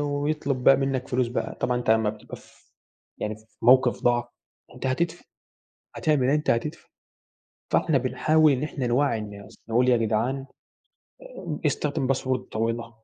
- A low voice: Yes, low, 130 Hz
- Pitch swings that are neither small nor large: Yes, average, 3.5 semitones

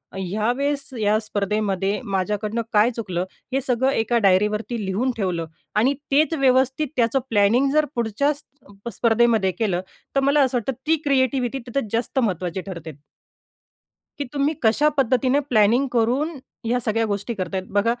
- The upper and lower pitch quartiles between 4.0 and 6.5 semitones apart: Yes, average, 4.5 semitones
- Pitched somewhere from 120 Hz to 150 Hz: No, high, 230 Hz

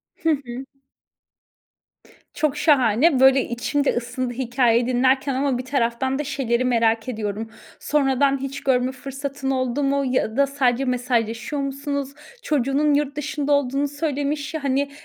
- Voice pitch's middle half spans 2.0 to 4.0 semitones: Yes, narrow, 2.4 semitones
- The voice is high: Yes, very high, 270 Hz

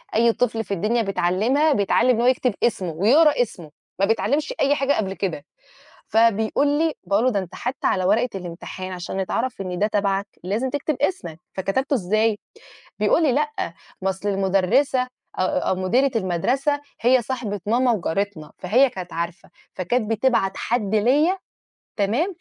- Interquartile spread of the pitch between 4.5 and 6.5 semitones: Yes, average, 5.2 semitones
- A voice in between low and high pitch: No, high, 220 Hz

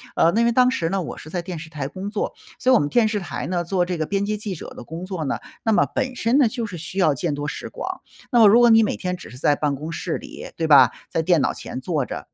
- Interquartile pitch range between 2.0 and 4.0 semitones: No, wide, 5.4 semitones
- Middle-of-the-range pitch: Yes, medium, 180 Hz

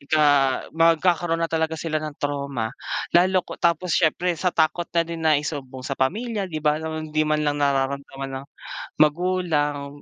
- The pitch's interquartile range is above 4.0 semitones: No, average, 2.9 semitones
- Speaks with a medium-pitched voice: Yes, medium, 155 Hz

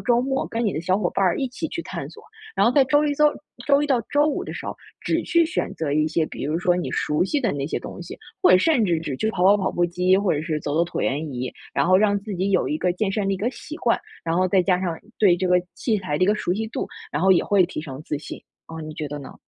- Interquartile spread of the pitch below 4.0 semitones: No, wide, 5.4 semitones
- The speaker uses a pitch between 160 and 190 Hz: Yes, medium, 185 Hz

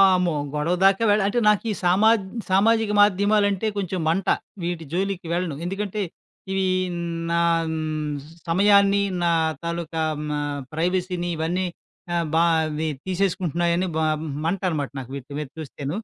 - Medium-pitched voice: Yes, medium, 180 Hz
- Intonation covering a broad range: No, average, 2.9 semitones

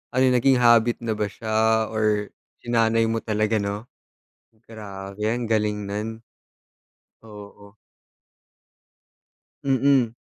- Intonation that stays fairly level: Yes, narrow, 1.9 semitones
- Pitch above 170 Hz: No, low, 110 Hz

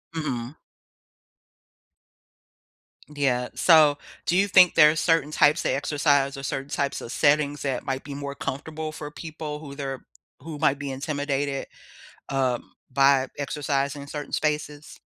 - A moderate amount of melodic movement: No, narrow, 1.8 semitones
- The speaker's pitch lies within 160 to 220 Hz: No, medium, 145 Hz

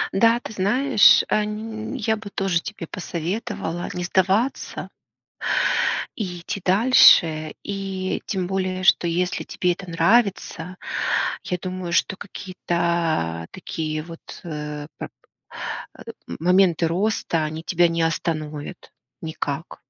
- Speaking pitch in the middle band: Yes, medium, 180 Hz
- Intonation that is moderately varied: Yes, average, 3.2 semitones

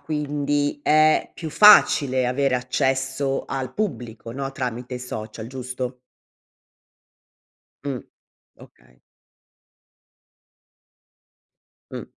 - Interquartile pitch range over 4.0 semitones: No, narrow, 2.4 semitones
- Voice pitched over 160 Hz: No, low, 130 Hz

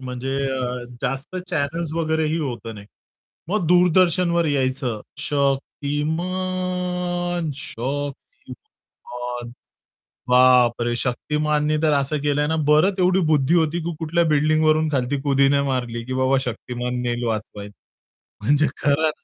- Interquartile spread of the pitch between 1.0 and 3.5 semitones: No, average, 4.3 semitones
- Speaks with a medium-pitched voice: Yes, medium, 145 Hz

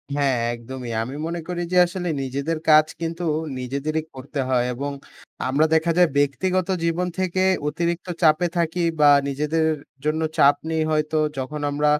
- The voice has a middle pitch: Yes, medium, 155 Hz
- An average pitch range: Yes, average, 3.3 semitones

